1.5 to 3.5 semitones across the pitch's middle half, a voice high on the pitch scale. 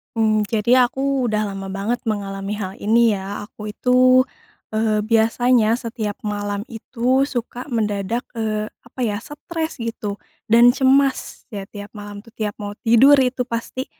Yes: average, 3.1 semitones; high, 225 Hz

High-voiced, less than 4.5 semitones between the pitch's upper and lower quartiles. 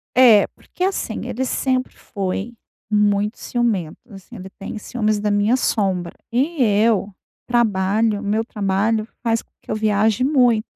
Yes: high, 215 Hz; average, 2.9 semitones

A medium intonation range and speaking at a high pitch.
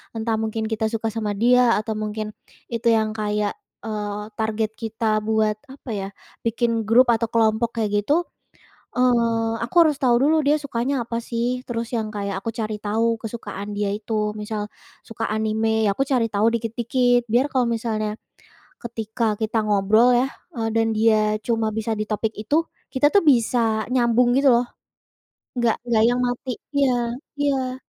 No: narrow, 2.0 semitones; high, 225 Hz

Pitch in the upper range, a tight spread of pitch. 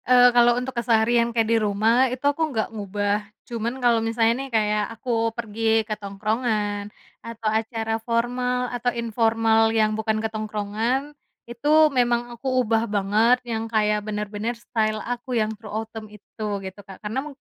Yes: high, 225 Hz; narrow, 2.0 semitones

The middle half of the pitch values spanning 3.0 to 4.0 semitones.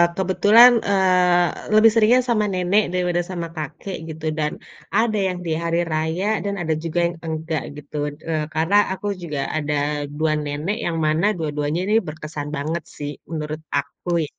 Yes: average, 3.5 semitones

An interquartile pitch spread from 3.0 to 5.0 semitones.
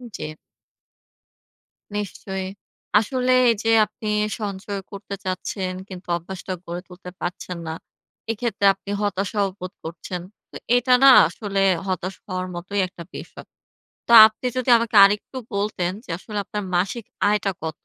No: narrow, 2.5 semitones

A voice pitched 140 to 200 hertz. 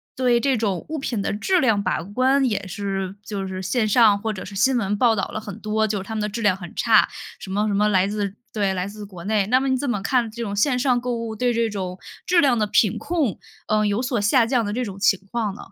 No: high, 215 Hz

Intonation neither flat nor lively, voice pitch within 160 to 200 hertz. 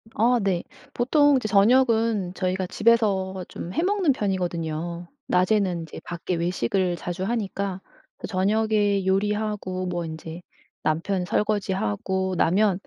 Yes: average, 3.3 semitones; high, 190 Hz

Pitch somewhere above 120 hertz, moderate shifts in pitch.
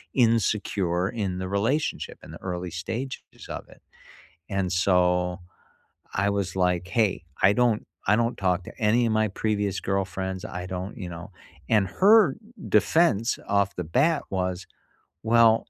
No: low, 100 Hz; average, 3.6 semitones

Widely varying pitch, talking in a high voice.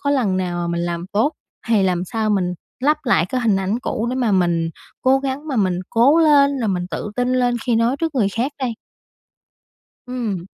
Yes: wide, 5.9 semitones; high, 230 Hz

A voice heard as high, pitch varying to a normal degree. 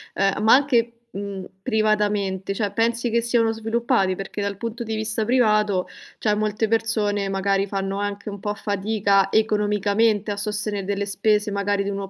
No: high, 210 Hz; narrow, 1.8 semitones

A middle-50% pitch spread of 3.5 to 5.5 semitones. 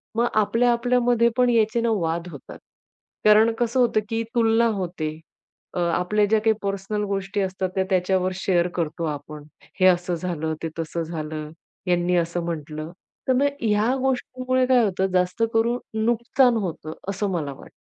Yes: average, 5.2 semitones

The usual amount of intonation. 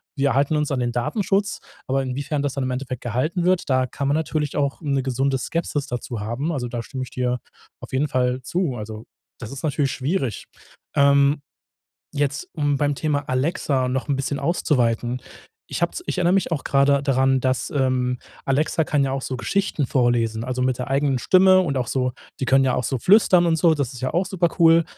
Yes: average, 3.0 semitones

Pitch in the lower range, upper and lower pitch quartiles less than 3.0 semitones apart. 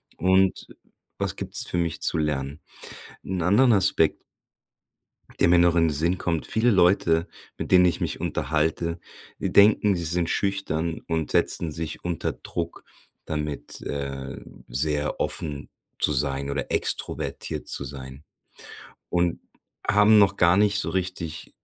No: very low, 85 Hz; average, 3.6 semitones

